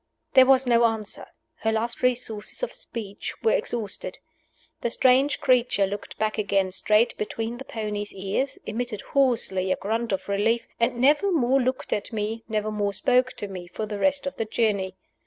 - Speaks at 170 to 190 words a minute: Yes, average, 175 wpm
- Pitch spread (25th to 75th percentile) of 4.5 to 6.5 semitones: No, average, 3.4 semitones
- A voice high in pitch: Yes, high, 225 Hz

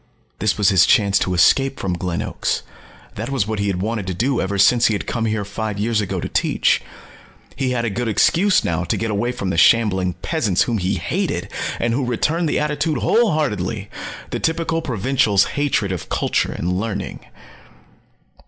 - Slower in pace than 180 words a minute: No, average, 190 wpm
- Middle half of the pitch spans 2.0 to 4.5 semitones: No, average, 5.0 semitones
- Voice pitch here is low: Yes, low, 110 Hz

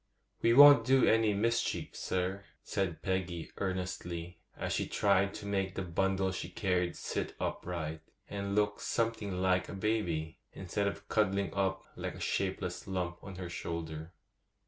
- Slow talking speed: No, average, 150 wpm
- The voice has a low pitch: Yes, very low, 95 Hz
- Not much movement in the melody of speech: Yes, narrow, 2.2 semitones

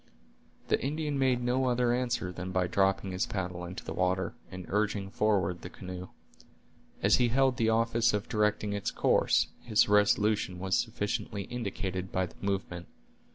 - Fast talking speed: No, average, 160 wpm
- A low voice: Yes, low, 100 Hz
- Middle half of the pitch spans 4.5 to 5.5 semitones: No, average, 4.1 semitones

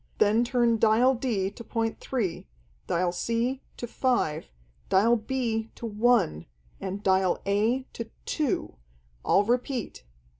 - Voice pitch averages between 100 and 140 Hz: No, high, 225 Hz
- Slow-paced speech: Yes, slow, 125 wpm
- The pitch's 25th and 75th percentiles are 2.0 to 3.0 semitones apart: No, average, 3.5 semitones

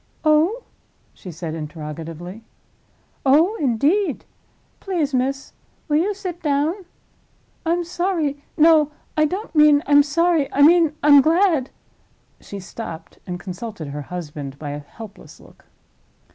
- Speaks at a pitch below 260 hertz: No, very high, 285 Hz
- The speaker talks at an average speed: No, slow, 120 wpm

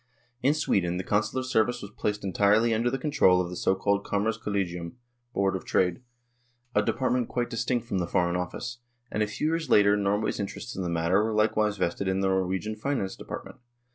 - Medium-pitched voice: No, low, 105 Hz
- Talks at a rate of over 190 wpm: Yes, average, 200 wpm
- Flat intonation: No, average, 3.5 semitones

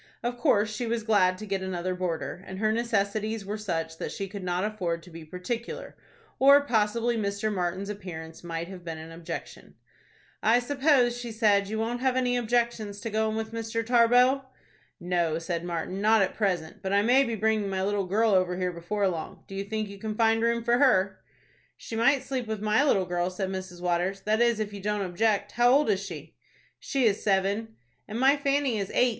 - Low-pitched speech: No, high, 210 Hz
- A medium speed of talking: No, fast, 210 wpm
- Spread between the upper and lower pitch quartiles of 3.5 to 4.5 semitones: Yes, average, 3.8 semitones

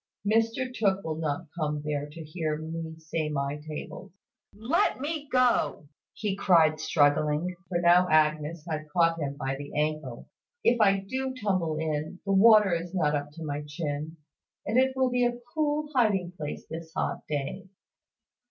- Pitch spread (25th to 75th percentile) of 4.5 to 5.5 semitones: Yes, average, 5.2 semitones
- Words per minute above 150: Yes, average, 165 wpm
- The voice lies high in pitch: No, medium, 165 Hz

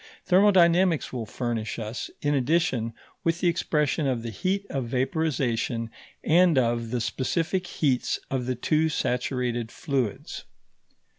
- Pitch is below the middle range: Yes, low, 130 Hz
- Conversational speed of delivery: No, slow, 130 wpm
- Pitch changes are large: Yes, wide, 5.8 semitones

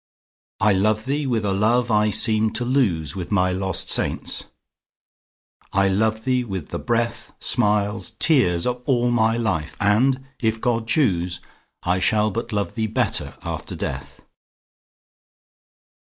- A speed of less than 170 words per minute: Yes, slow, 135 wpm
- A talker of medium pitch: No, low, 110 Hz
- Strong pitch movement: No, average, 3.8 semitones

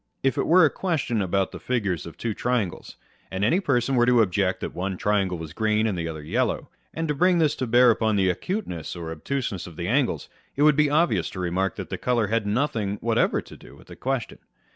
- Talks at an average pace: No, fast, 225 wpm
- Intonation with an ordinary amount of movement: No, wide, 6.3 semitones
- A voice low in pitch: Yes, low, 110 Hz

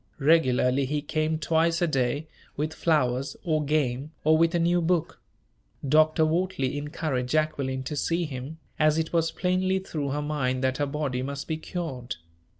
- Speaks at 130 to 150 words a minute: No, average, 165 wpm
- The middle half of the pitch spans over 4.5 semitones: No, average, 3.2 semitones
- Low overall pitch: No, medium, 155 Hz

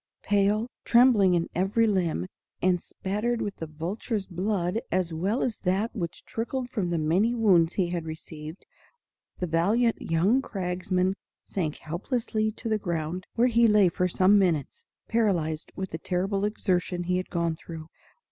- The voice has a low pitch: No, medium, 185 Hz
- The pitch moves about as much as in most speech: Yes, average, 4.0 semitones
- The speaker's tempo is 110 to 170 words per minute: Yes, average, 155 wpm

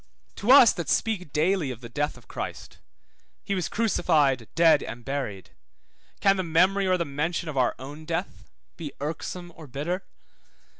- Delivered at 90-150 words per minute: No, average, 165 wpm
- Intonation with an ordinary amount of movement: Yes, average, 4.6 semitones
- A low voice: No, medium, 165 Hz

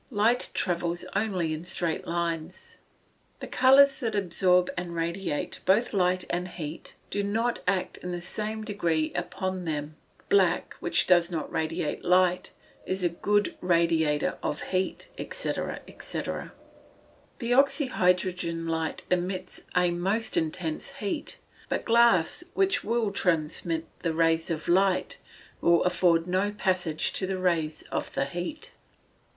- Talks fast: No, average, 140 wpm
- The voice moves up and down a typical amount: Yes, average, 3.4 semitones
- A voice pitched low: No, medium, 180 Hz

